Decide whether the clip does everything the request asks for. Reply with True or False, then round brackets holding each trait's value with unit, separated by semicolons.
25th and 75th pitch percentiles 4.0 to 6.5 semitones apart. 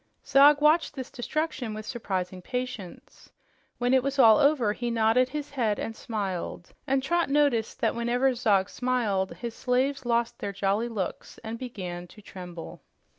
True (4.3 semitones)